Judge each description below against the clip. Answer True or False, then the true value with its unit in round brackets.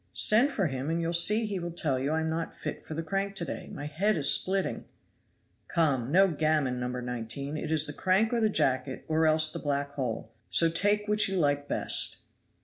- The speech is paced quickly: True (220 wpm)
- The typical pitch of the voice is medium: True (160 Hz)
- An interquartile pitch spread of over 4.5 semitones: True (5.2 semitones)